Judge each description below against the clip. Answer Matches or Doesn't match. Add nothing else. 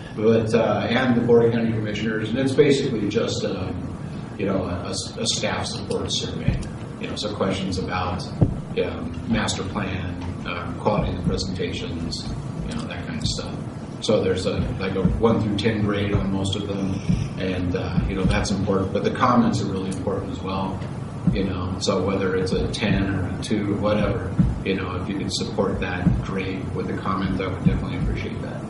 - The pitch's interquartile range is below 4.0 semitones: Matches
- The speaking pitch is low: Matches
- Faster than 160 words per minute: Matches